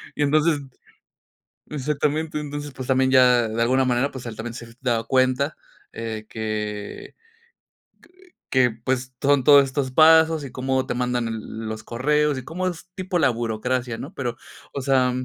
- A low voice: Yes, low, 130 Hz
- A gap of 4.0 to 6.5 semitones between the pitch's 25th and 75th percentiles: No, average, 3.5 semitones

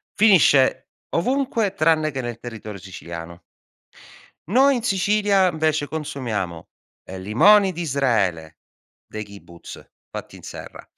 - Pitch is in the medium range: Yes, medium, 145 Hz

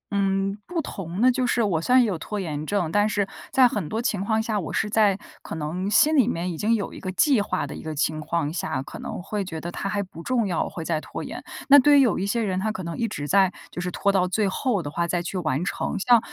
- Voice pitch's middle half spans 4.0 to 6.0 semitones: Yes, average, 4.4 semitones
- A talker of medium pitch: No, high, 195 Hz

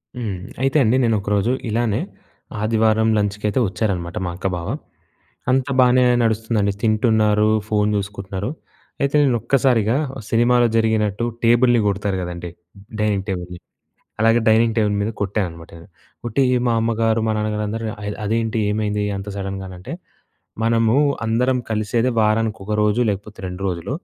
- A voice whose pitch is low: Yes, low, 110 Hz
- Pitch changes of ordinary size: No, narrow, 2.3 semitones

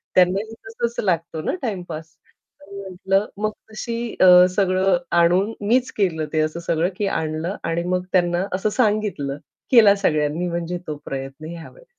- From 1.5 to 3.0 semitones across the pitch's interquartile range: No, average, 3.6 semitones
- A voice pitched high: No, medium, 180 Hz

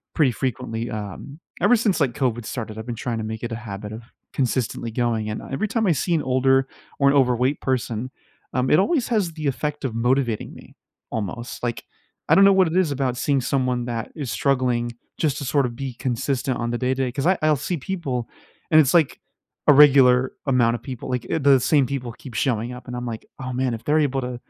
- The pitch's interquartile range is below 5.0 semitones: Yes, average, 3.0 semitones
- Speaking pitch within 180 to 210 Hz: No, low, 130 Hz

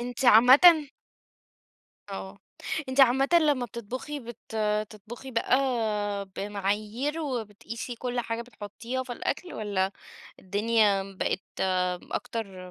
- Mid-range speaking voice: No, high, 230 Hz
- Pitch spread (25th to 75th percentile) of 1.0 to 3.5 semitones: No, average, 3.9 semitones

